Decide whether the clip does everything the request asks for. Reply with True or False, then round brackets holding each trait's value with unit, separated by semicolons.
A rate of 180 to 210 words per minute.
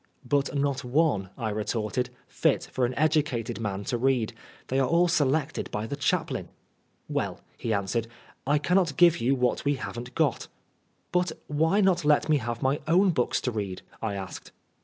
True (190 wpm)